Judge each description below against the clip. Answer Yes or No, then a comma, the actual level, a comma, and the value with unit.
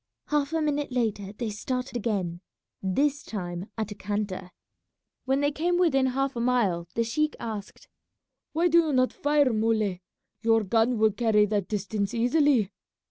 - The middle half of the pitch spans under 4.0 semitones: No, average, 5.0 semitones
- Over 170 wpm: No, average, 160 wpm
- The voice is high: Yes, high, 230 Hz